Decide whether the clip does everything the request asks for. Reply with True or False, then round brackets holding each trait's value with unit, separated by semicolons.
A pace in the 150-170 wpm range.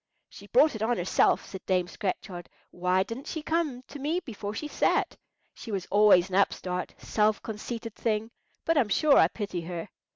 False (185 wpm)